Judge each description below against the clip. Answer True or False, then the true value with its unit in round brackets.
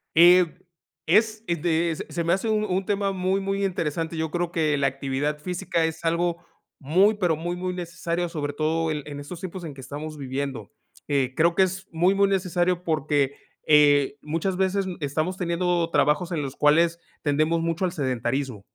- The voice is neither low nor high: True (165 Hz)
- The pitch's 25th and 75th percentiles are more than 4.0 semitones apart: False (3.4 semitones)